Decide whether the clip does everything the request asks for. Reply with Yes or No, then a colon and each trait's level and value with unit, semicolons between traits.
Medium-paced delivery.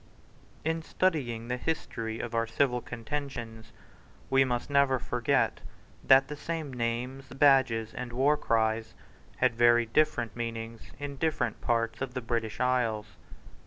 No: slow, 130 wpm